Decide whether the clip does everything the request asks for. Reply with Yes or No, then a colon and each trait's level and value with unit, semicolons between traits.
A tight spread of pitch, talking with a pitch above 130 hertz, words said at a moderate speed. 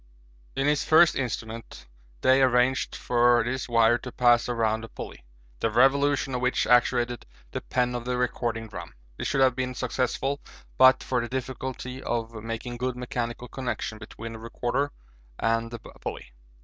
No: narrow, 2.0 semitones; low, 125 Hz; average, 160 wpm